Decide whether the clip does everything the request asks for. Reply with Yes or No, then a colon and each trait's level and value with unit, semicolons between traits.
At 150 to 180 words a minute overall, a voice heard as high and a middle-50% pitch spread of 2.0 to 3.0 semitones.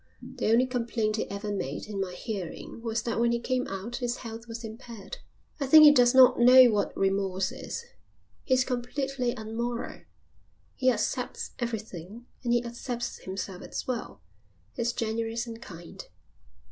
Yes: average, 160 wpm; high, 235 Hz; narrow, 2.6 semitones